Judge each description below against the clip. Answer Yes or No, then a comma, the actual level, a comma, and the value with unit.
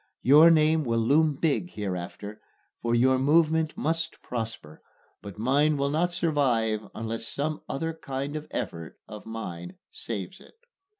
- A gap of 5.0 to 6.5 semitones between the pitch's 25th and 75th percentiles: Yes, wide, 5.6 semitones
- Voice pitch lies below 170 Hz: Yes, low, 135 Hz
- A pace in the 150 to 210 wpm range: No, average, 140 wpm